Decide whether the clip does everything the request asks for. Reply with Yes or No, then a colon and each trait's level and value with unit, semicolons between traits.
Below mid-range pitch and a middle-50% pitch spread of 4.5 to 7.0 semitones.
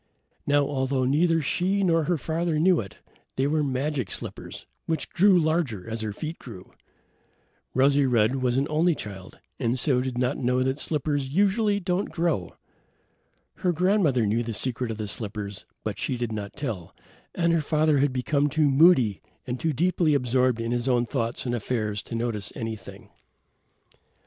Yes: low, 130 Hz; average, 5.3 semitones